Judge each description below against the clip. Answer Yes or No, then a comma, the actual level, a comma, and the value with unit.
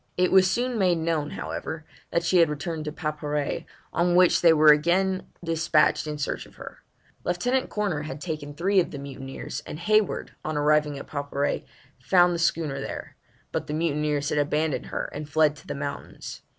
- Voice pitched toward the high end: No, medium, 155 Hz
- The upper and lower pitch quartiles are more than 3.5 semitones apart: No, average, 3.0 semitones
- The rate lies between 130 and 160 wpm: No, average, 185 wpm